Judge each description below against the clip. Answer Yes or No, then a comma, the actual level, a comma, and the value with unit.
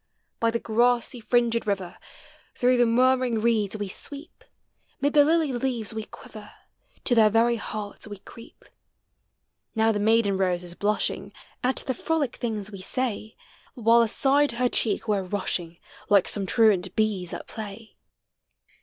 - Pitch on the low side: No, high, 225 Hz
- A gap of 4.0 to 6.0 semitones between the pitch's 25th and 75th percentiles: No, average, 3.1 semitones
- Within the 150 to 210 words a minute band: Yes, average, 155 wpm